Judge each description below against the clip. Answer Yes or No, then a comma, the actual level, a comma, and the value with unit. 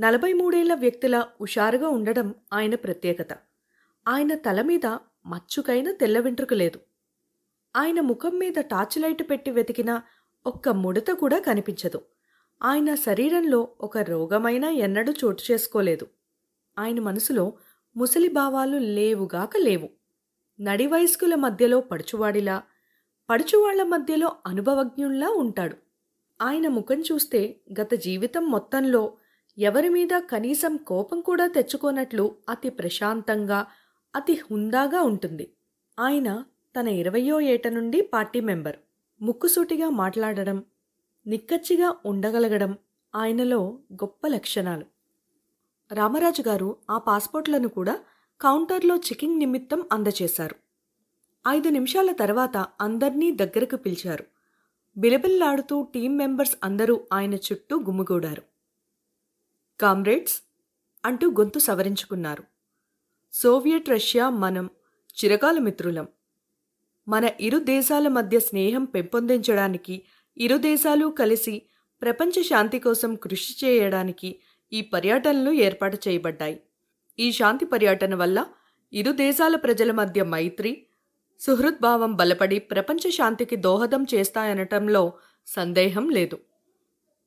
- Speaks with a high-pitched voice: Yes, high, 235 Hz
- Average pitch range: No, wide, 5.9 semitones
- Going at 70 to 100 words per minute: Yes, average, 95 wpm